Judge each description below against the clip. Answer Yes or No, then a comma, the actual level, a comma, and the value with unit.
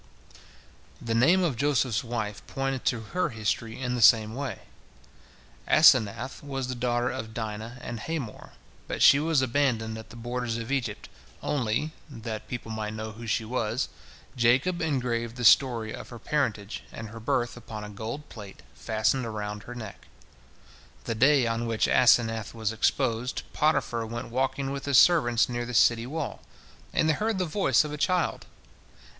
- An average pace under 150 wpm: No, average, 165 wpm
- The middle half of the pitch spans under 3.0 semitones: No, average, 3.3 semitones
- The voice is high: No, low, 120 Hz